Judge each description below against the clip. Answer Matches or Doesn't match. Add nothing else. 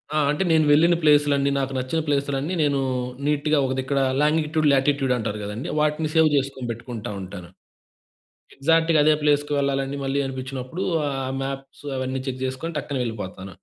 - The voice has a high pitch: Doesn't match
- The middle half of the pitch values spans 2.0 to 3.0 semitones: Matches